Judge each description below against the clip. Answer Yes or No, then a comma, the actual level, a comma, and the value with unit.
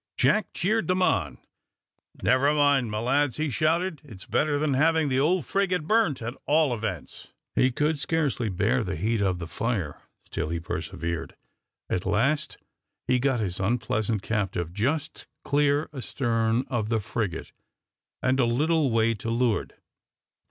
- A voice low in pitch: Yes, low, 125 Hz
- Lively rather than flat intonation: Yes, wide, 5.9 semitones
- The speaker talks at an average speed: Yes, average, 150 wpm